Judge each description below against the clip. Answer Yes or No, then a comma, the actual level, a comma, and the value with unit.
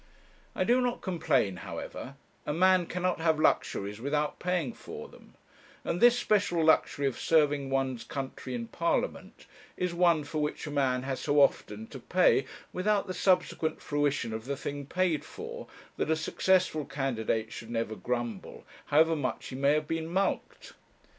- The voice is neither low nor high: Yes, medium, 150 Hz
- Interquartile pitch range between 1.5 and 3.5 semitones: No, average, 4.9 semitones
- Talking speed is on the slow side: No, average, 165 wpm